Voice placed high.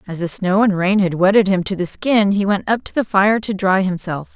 Yes: high, 195 Hz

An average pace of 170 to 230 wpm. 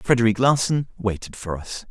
No: average, 155 wpm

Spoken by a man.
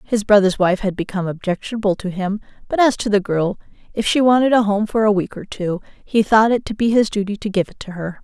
No: female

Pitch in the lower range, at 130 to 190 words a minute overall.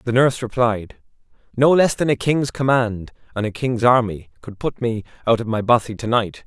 No: low, 115 Hz; fast, 205 wpm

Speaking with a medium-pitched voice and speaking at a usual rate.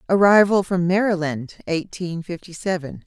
No: medium, 180 Hz; slow, 120 wpm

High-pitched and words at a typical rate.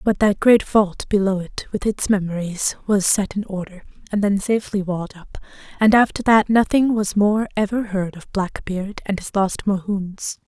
Yes: high, 200 Hz; average, 185 wpm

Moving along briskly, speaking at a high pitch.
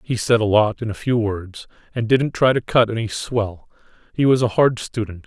No: fast, 230 wpm; low, 115 Hz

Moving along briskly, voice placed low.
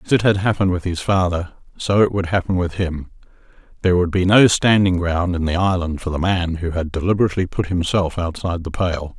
Yes: fast, 210 wpm; very low, 90 Hz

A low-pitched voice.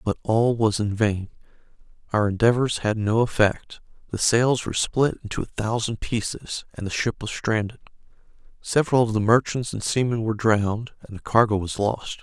Yes: low, 110 Hz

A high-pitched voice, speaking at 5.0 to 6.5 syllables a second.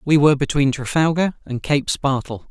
No: medium, 140 Hz; 5.1 syllables/s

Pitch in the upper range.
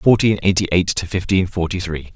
No: very low, 90 Hz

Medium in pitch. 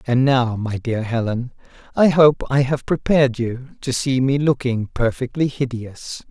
No: low, 130 Hz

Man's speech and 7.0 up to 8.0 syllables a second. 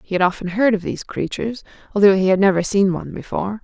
No: female; 7.1 syllables/s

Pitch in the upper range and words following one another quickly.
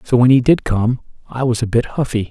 No: low, 120 Hz; fast, 260 wpm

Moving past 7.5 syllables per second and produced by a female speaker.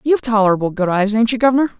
Yes: 8.0 syllables/s; female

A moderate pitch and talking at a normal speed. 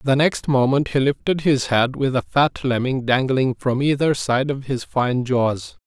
No: low, 130 Hz; average, 195 wpm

